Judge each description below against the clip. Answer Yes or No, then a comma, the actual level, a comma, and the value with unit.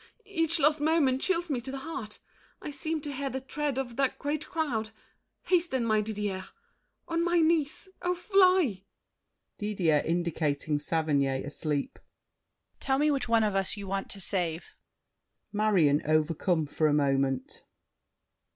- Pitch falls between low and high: No, high, 230 Hz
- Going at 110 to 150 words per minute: Yes, average, 140 wpm